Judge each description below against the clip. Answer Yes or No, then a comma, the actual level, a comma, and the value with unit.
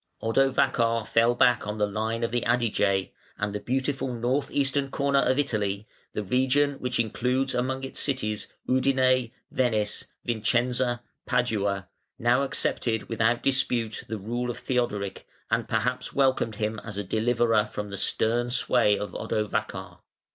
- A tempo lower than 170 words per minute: Yes, average, 145 wpm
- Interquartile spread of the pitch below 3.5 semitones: Yes, average, 3.1 semitones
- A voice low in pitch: Yes, low, 120 Hz